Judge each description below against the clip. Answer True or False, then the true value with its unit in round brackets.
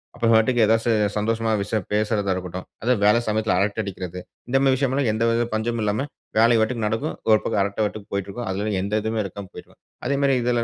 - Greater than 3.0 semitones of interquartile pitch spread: False (2.5 semitones)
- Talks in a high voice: False (110 Hz)